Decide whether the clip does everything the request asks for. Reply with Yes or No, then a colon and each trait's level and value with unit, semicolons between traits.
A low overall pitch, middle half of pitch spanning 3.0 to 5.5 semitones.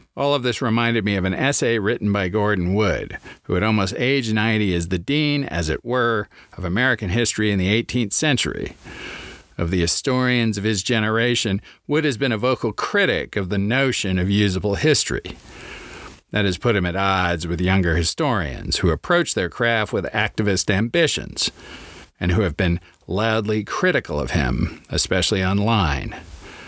Yes: low, 105 Hz; average, 4.1 semitones